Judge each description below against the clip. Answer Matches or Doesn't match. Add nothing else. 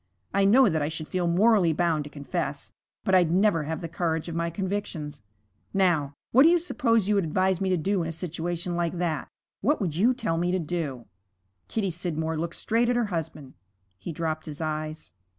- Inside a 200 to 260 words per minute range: Matches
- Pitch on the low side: Doesn't match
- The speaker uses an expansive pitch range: Doesn't match